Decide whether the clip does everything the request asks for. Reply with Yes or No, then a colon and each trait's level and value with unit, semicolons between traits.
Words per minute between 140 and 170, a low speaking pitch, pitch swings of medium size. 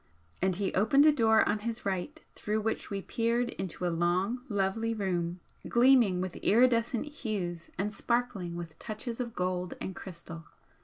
No: average, 160 wpm; high, 210 Hz; average, 4.5 semitones